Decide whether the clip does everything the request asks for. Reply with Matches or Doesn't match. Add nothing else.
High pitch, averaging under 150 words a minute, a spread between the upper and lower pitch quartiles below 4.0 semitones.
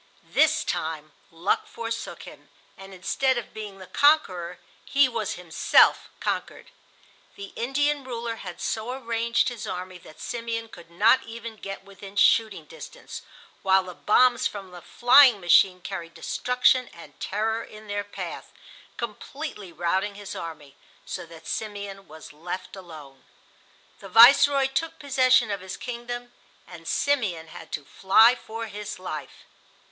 Doesn't match